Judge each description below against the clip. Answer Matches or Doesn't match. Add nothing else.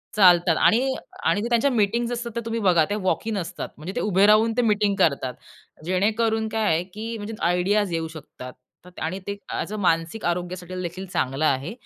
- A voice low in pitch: Doesn't match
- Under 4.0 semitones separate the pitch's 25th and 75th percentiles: Doesn't match